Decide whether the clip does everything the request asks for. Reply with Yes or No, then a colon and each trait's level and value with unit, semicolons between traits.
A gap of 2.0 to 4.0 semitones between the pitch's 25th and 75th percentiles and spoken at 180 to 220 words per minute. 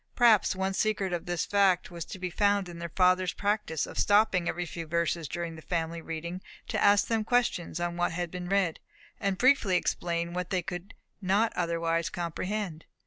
Yes: average, 2.9 semitones; average, 195 wpm